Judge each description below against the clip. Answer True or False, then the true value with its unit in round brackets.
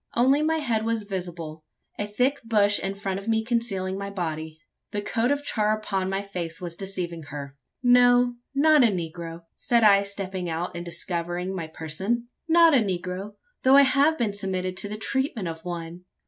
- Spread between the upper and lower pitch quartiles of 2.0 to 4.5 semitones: False (5.0 semitones)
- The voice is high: True (200 Hz)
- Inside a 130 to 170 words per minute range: False (185 wpm)